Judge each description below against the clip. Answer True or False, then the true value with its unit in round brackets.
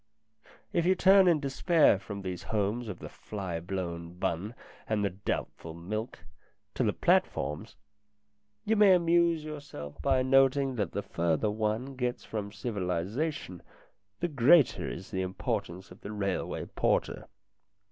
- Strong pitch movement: True (7.3 semitones)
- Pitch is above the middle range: False (110 Hz)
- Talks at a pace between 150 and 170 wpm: False (140 wpm)